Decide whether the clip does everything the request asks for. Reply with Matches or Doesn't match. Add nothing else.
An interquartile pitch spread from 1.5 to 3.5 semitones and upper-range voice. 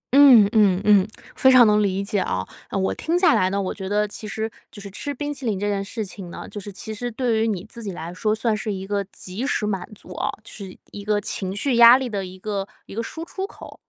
Matches